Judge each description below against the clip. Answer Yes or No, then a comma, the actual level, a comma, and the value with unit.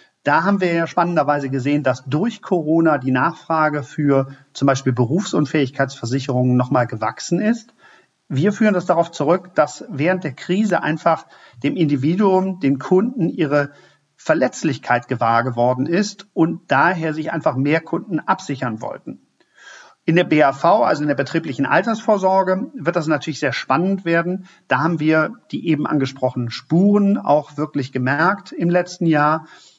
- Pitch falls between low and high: Yes, medium, 155 Hz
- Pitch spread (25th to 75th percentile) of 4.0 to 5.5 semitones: Yes, average, 4.5 semitones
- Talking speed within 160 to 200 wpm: No, average, 145 wpm